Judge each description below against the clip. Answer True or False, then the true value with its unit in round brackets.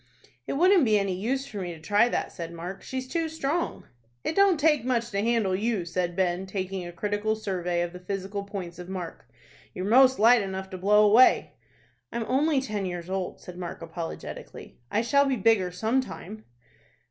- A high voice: True (205 Hz)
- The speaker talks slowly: False (195 wpm)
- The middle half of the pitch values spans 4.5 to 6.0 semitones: True (5.2 semitones)